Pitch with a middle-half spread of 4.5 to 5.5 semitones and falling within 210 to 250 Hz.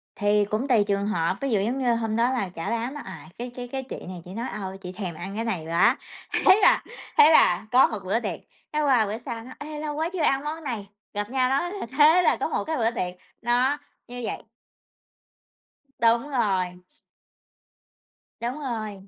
Yes: average, 4.8 semitones; high, 235 Hz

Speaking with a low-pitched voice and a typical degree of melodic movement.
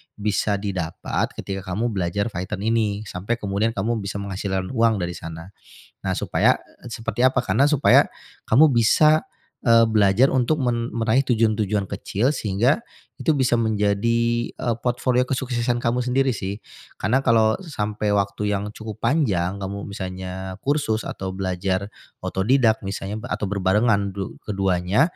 Yes: low, 105 Hz; average, 3.5 semitones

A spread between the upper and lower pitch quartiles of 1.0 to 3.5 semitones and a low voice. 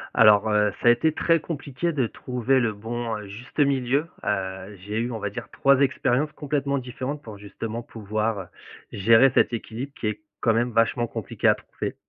No: average, 4.0 semitones; low, 120 Hz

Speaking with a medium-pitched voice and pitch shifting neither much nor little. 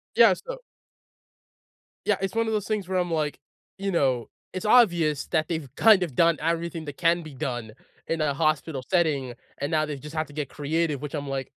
Yes: medium, 160 Hz; average, 3.4 semitones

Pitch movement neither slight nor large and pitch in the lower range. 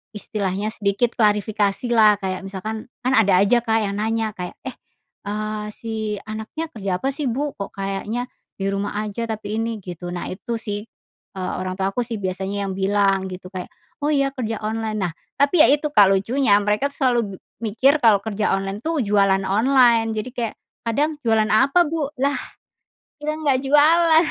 No: average, 4.1 semitones; high, 215 Hz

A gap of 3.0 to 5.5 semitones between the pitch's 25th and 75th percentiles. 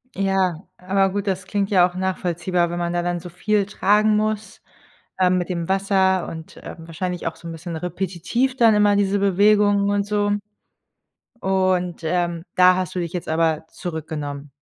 No: narrow, 2.5 semitones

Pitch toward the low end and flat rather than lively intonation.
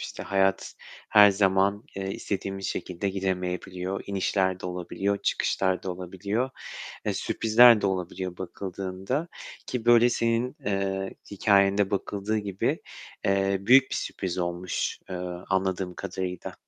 Yes: very low, 95 Hz; narrow, 1.6 semitones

